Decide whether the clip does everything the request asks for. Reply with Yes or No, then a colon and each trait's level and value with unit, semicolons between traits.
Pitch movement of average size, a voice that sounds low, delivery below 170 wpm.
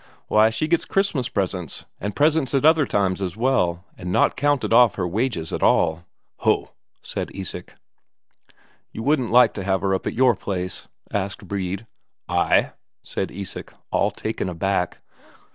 No: wide, 5.7 semitones; low, 100 Hz; average, 155 wpm